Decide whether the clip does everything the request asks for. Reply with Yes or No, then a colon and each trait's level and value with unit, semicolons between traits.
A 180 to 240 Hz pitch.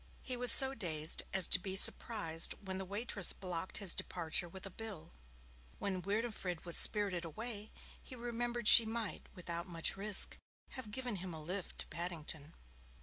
Yes: high, 190 Hz